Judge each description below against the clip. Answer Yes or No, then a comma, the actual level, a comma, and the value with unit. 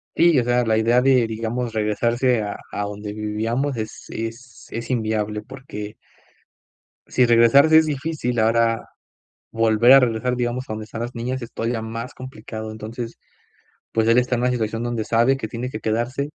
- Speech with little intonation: Yes, narrow, 2.3 semitones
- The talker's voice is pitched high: No, low, 115 Hz